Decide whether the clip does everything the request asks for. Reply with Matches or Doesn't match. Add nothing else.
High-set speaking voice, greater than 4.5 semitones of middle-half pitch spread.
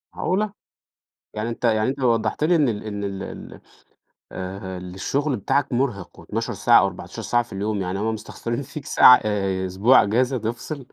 Doesn't match